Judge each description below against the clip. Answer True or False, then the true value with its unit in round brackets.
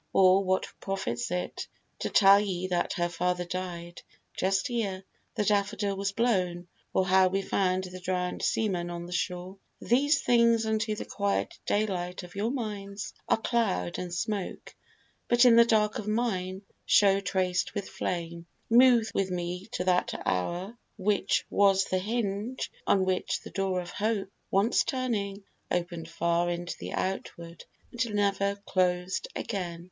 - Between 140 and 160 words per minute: True (155 wpm)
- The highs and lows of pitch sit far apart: False (2.8 semitones)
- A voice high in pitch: True (195 Hz)